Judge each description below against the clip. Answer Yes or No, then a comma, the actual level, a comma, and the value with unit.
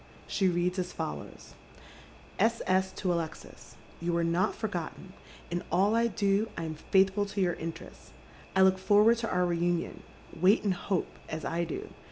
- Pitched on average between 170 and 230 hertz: Yes, medium, 185 Hz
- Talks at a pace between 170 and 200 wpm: Yes, average, 180 wpm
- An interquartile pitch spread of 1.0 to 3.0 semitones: Yes, average, 2.7 semitones